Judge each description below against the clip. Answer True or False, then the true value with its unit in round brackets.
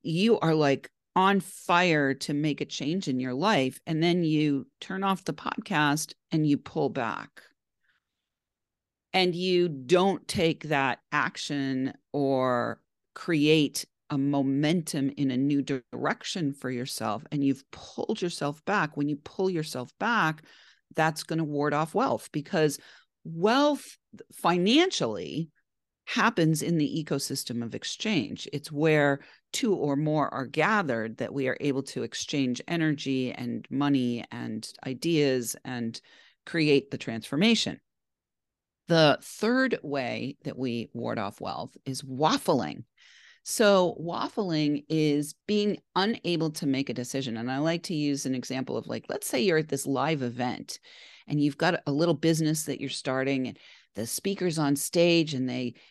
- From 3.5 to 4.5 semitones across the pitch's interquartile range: True (3.8 semitones)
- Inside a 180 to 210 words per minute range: False (145 wpm)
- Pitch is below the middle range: False (150 Hz)